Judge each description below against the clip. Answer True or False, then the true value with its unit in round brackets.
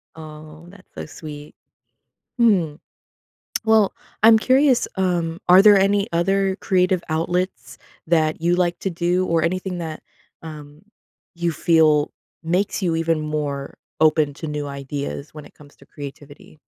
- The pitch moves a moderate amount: True (3.4 semitones)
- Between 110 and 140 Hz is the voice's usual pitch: False (165 Hz)